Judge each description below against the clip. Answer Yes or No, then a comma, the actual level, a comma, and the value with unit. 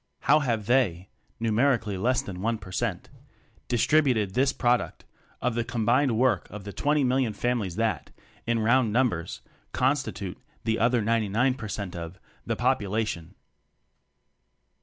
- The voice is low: Yes, low, 115 Hz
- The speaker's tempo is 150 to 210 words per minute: No, average, 140 wpm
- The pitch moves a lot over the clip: No, average, 3.5 semitones